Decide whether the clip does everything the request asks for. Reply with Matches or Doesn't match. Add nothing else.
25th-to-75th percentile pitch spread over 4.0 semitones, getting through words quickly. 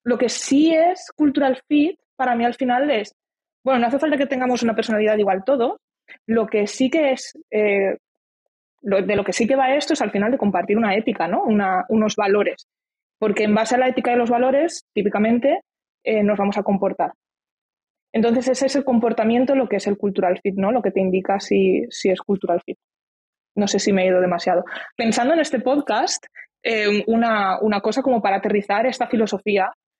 Matches